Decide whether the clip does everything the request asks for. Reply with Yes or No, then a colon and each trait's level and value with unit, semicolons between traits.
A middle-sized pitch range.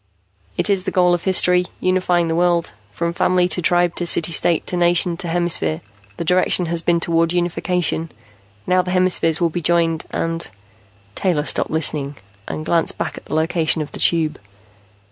No: narrow, 1.6 semitones